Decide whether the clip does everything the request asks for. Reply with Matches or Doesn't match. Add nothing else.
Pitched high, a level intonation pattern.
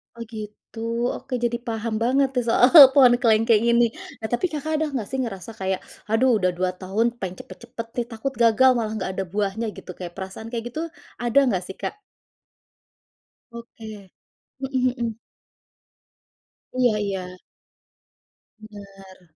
Doesn't match